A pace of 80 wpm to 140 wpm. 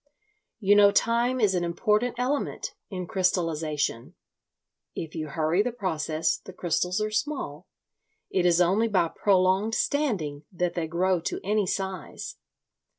Yes: slow, 135 wpm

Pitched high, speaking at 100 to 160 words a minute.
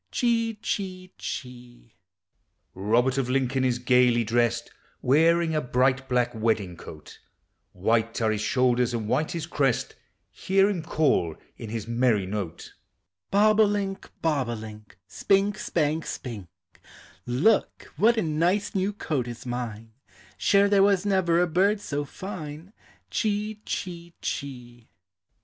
No: low, 135 Hz; slow, 135 wpm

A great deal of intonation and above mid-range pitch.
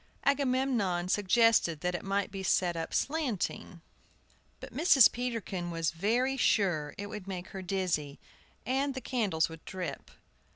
Yes: wide, 6.1 semitones; high, 195 Hz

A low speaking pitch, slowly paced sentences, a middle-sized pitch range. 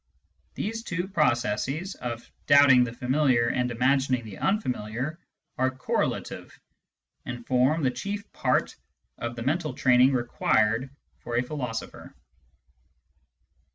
Yes: low, 130 Hz; slow, 115 wpm; average, 4.0 semitones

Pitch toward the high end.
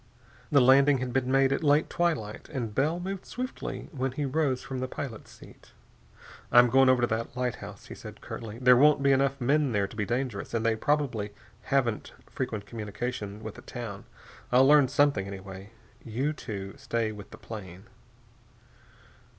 No: low, 125 Hz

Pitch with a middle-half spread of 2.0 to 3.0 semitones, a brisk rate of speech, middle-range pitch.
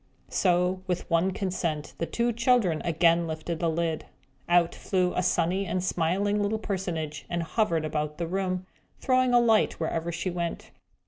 No: average, 2.7 semitones; average, 165 wpm; medium, 175 Hz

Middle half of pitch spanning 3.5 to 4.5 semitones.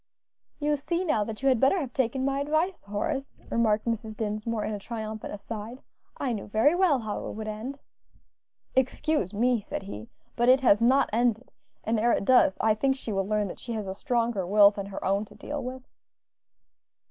Yes: average, 4.0 semitones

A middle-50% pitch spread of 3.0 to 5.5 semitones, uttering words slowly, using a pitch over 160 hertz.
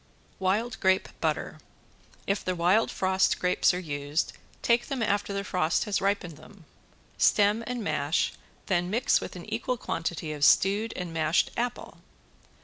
No: average, 3.8 semitones; average, 150 wpm; high, 190 Hz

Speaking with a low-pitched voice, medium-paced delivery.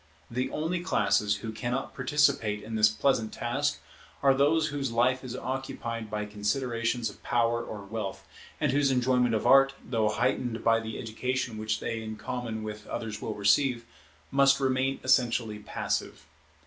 Yes: low, 120 Hz; average, 160 wpm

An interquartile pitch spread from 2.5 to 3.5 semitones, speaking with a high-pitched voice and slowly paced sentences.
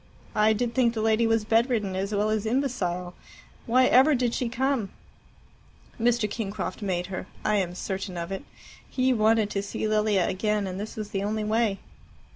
No: average, 3.0 semitones; high, 215 Hz; average, 180 wpm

